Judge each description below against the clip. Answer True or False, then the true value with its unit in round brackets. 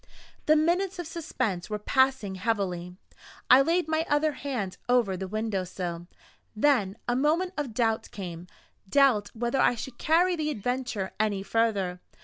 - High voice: True (230 Hz)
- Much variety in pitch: True (7.1 semitones)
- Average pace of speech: True (150 wpm)